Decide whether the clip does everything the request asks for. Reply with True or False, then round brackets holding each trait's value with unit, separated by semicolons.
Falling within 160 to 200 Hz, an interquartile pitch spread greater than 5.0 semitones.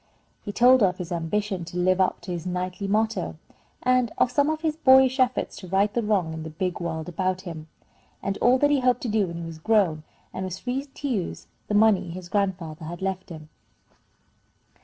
True (190 Hz; 5.6 semitones)